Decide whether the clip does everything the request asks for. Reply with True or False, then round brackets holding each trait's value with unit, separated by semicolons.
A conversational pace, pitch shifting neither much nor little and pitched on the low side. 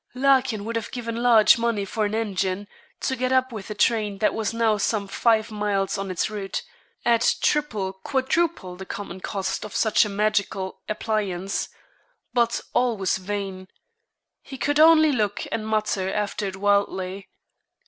False (160 wpm; 3.0 semitones; 210 Hz)